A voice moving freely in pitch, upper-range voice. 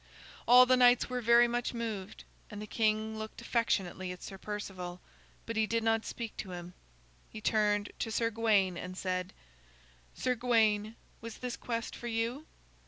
No: narrow, 2.4 semitones; high, 220 Hz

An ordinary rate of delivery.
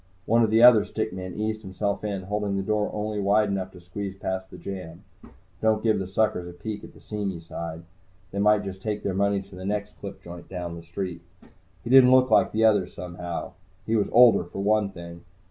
No: fast, 220 wpm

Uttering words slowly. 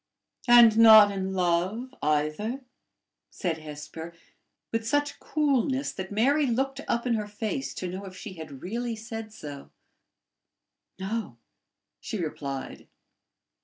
Yes: slow, 125 wpm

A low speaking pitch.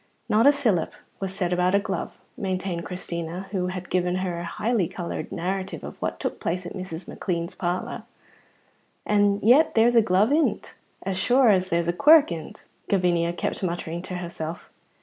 No: medium, 185 Hz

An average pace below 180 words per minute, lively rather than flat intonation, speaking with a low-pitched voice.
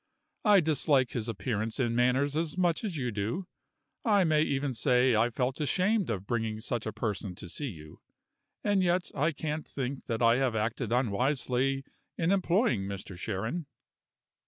Yes: average, 170 wpm; wide, 5.9 semitones; low, 130 Hz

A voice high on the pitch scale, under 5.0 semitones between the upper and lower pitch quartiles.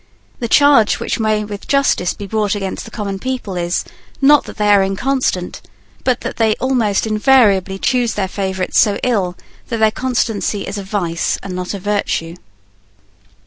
Yes: high, 210 Hz; average, 3.5 semitones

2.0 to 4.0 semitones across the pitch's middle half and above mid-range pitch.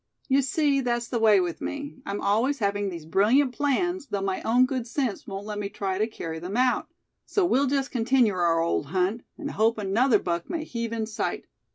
No: average, 5.2 semitones; high, 225 Hz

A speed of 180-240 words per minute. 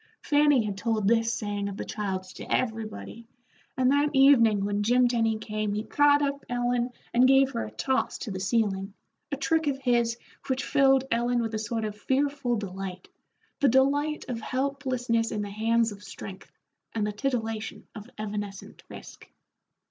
No: average, 170 wpm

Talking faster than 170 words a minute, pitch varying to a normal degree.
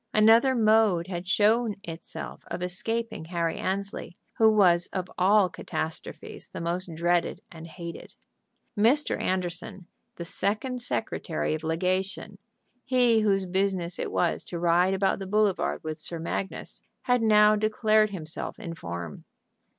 No: slow, 135 wpm; average, 3.9 semitones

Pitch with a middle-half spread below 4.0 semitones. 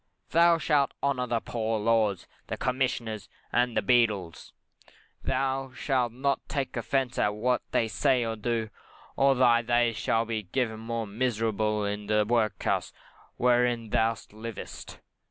Yes: narrow, 2.5 semitones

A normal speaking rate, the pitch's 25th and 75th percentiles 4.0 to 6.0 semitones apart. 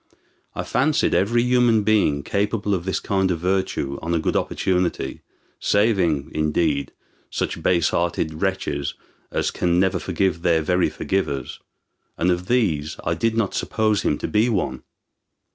Yes: average, 150 wpm; average, 4.3 semitones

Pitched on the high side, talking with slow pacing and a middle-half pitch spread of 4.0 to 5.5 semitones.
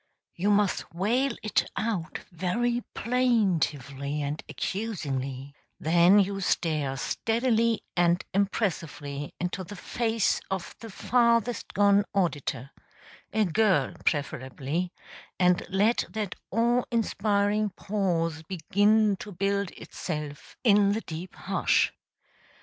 Yes: high, 195 Hz; slow, 105 wpm; average, 5.0 semitones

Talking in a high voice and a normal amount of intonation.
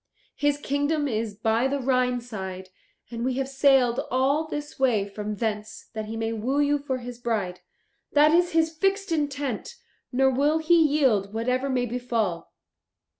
Yes: very high, 255 Hz; average, 4.4 semitones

